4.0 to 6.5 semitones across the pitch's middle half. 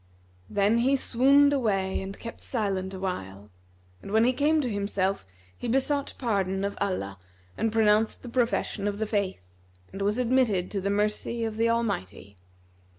No: average, 3.4 semitones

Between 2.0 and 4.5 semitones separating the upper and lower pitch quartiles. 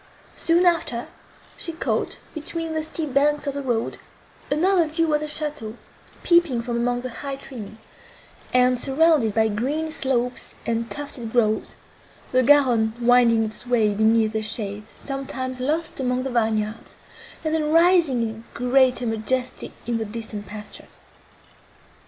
No: average, 4.9 semitones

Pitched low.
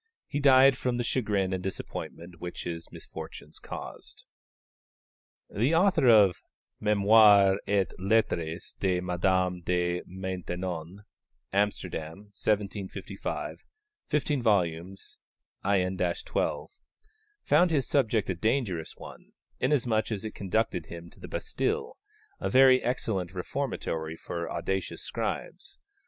Yes: low, 100 Hz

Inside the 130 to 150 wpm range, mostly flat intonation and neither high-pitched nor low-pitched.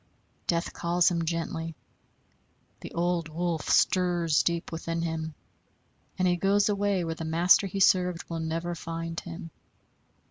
Yes: average, 140 wpm; narrow, 1.4 semitones; medium, 170 Hz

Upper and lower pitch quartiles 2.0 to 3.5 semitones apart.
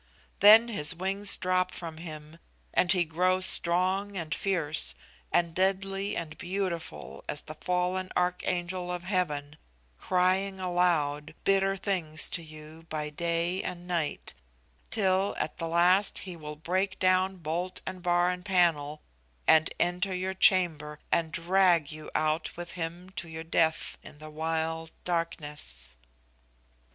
Yes: average, 2.8 semitones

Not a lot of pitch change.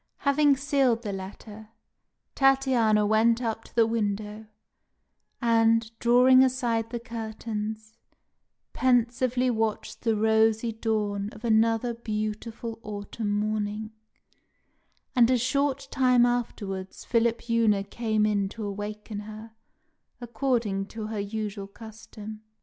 Yes: narrow, 2.1 semitones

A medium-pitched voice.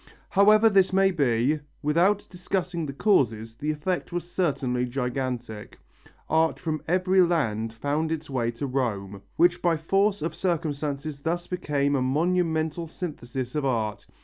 Yes: medium, 155 Hz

